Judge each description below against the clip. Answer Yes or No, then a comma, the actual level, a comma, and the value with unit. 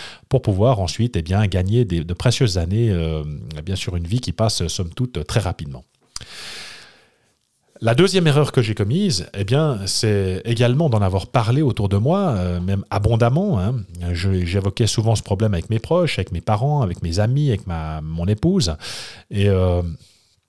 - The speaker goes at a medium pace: Yes, average, 180 wpm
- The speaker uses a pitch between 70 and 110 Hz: Yes, low, 105 Hz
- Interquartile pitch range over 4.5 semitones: Yes, average, 5.1 semitones